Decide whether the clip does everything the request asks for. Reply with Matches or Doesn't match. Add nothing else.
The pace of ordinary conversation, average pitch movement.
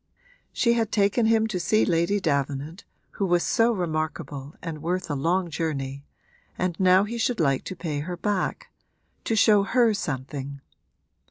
Doesn't match